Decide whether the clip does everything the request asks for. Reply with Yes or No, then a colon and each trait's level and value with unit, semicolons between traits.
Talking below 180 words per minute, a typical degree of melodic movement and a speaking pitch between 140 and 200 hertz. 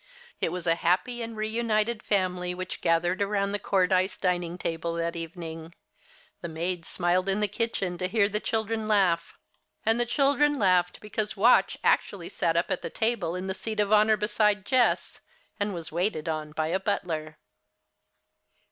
Yes: average, 170 wpm; average, 3.9 semitones; high, 190 Hz